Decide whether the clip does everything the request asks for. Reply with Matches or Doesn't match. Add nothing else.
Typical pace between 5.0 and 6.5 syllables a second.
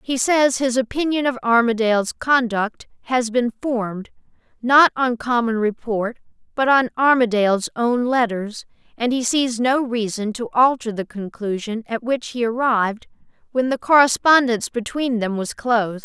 Doesn't match